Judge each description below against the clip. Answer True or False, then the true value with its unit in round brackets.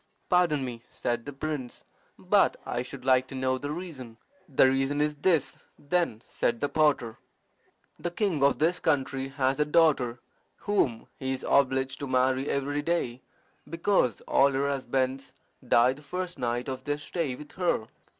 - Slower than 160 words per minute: False (165 wpm)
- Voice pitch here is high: False (135 Hz)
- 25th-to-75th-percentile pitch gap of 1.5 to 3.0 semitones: True (2.7 semitones)